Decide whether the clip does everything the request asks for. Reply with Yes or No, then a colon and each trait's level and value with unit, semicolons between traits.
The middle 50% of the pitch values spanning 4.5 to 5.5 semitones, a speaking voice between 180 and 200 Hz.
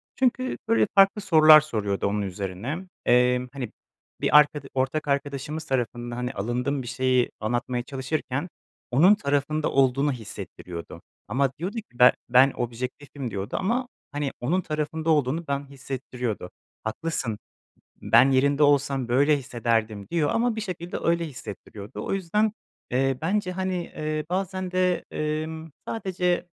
No: average, 5.0 semitones; medium, 140 Hz